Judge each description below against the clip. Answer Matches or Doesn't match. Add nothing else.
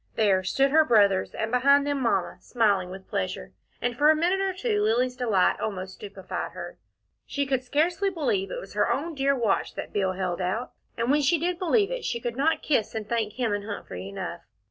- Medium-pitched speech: Doesn't match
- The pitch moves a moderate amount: Doesn't match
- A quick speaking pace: Matches